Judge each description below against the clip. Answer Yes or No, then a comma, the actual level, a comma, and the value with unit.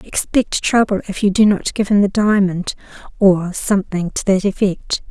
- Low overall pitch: No, high, 195 Hz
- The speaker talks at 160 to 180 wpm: Yes, average, 175 wpm